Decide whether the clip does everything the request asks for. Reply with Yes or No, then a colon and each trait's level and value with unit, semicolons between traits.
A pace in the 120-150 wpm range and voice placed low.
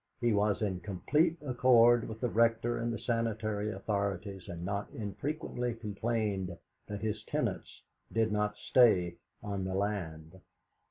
Yes: average, 140 wpm; low, 105 Hz